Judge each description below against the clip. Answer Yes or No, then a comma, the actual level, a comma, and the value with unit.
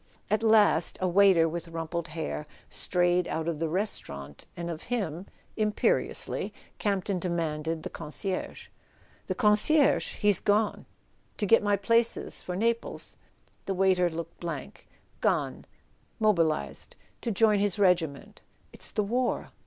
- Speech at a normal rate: No, slow, 130 wpm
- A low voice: No, medium, 185 Hz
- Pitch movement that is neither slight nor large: Yes, average, 4.0 semitones